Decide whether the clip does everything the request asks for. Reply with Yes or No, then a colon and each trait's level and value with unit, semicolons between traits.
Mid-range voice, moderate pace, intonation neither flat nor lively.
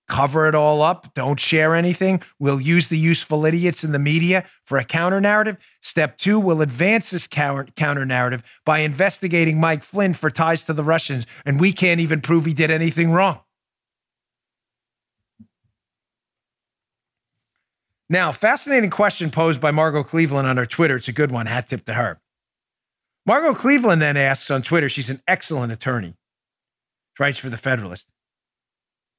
Yes: medium, 155 Hz; average, 155 wpm; average, 3.8 semitones